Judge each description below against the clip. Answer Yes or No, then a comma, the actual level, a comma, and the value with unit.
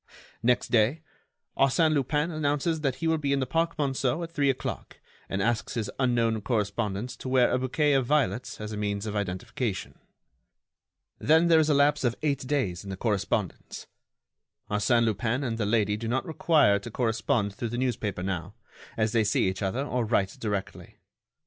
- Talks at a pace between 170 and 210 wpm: Yes, average, 180 wpm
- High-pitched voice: No, low, 120 Hz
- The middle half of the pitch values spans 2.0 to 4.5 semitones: No, average, 5.2 semitones